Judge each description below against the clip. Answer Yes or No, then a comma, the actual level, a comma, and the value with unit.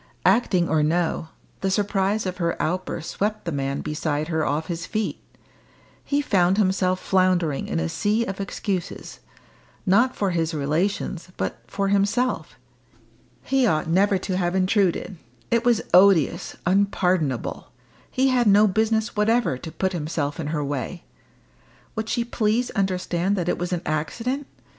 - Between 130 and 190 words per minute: Yes, average, 150 wpm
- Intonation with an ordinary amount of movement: Yes, average, 4.3 semitones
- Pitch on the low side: No, medium, 185 Hz